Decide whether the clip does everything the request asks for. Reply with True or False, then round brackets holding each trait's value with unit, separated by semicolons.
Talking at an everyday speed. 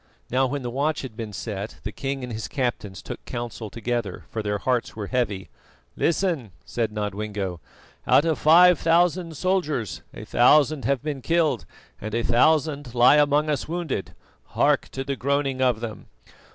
True (165 wpm)